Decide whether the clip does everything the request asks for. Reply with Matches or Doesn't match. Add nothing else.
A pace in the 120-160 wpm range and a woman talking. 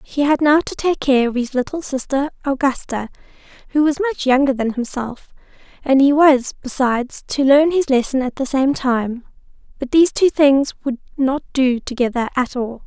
Doesn't match